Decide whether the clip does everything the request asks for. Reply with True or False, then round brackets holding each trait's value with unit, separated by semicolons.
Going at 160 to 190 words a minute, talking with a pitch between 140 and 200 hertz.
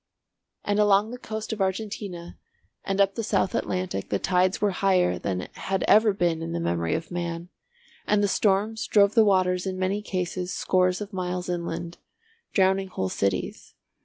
True (170 wpm; 185 Hz)